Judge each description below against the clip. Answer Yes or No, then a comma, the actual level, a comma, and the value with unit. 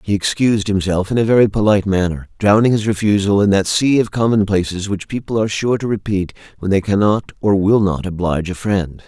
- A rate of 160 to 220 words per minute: Yes, fast, 205 wpm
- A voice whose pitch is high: No, low, 100 Hz